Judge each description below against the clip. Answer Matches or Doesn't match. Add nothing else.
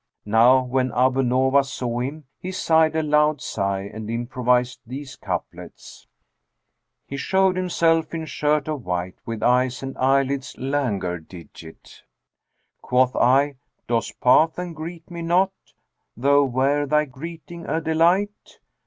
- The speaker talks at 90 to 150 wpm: Matches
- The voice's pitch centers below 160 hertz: Matches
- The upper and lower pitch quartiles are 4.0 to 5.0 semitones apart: Matches